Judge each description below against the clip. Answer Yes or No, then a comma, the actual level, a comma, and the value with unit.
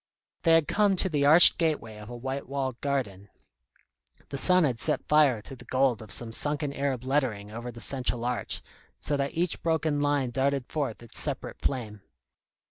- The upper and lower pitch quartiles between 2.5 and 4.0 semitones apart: Yes, average, 3.7 semitones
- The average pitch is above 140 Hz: No, low, 135 Hz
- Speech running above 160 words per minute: Yes, average, 185 wpm